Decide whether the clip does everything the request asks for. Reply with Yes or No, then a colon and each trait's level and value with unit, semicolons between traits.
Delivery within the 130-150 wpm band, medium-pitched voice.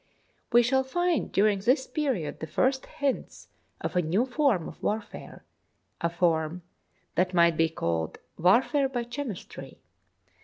No: average, 145 wpm; high, 215 Hz